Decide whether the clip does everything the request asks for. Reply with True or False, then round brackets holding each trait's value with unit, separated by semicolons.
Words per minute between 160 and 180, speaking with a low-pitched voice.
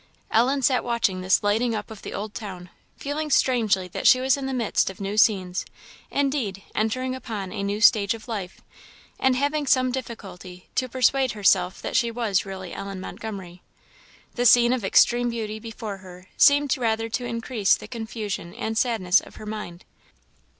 False (175 wpm; 220 Hz)